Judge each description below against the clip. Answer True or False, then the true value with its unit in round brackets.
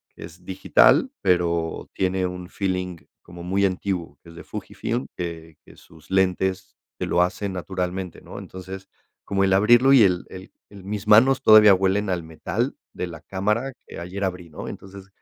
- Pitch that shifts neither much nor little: False (2.0 semitones)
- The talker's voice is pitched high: False (95 Hz)